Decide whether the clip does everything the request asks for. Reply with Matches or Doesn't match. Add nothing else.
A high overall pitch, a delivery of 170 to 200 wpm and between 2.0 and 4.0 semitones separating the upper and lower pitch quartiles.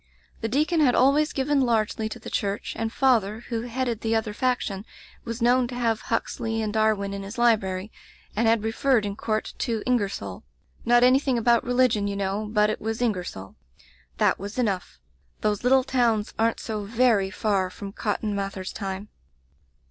Matches